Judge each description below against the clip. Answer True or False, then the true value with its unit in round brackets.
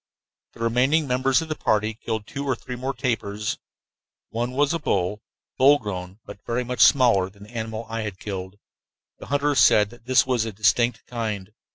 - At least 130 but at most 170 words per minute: False (190 wpm)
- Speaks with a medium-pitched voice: False (115 Hz)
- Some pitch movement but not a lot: True (3.6 semitones)